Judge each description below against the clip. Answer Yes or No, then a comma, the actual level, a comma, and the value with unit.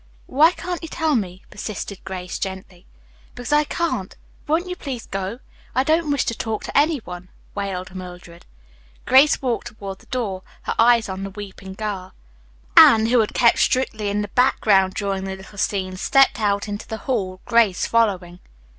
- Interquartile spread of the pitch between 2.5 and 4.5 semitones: No, average, 4.9 semitones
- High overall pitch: Yes, high, 210 Hz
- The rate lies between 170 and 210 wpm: Yes, average, 175 wpm